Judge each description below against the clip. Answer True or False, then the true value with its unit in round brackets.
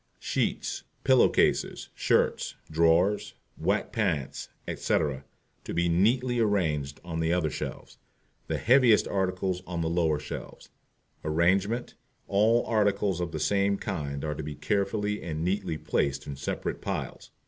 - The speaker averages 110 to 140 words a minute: True (135 wpm)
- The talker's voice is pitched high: False (90 Hz)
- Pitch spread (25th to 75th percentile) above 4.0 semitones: True (4.7 semitones)